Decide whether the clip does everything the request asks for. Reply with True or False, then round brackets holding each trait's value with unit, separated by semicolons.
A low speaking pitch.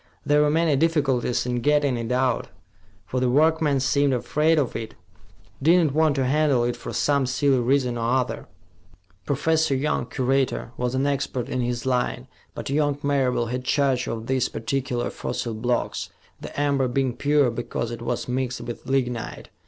True (130 Hz)